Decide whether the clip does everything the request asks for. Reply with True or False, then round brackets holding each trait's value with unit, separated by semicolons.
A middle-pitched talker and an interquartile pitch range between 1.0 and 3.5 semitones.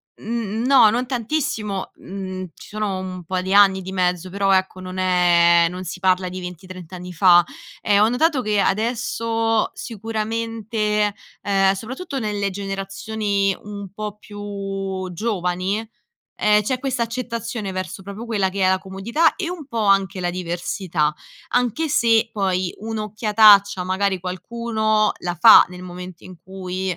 False (200 Hz; 3.1 semitones)